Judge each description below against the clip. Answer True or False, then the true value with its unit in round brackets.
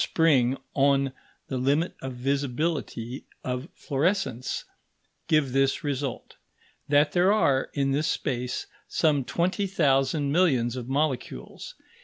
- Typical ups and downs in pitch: True (3.1 semitones)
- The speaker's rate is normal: False (115 wpm)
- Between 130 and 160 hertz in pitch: True (140 Hz)